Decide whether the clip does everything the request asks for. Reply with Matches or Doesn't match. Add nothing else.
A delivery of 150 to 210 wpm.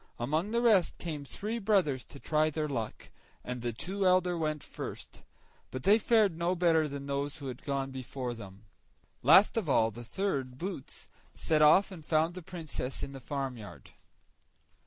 Matches